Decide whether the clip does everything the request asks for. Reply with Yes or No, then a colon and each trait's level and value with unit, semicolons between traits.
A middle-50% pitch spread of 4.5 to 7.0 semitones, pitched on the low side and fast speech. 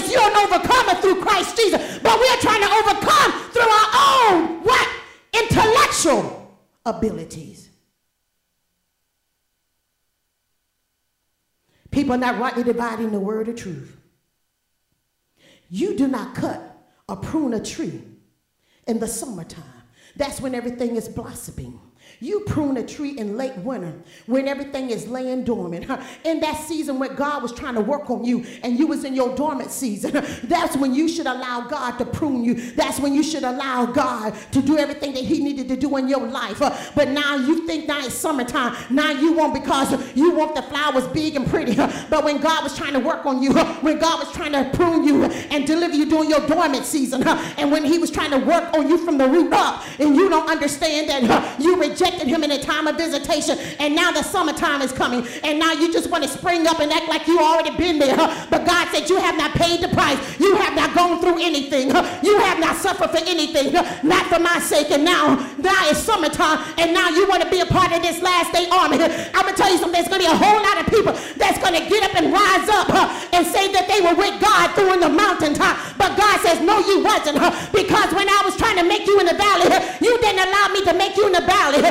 No: average, 5.0 semitones; very high, 310 Hz; fast, 210 wpm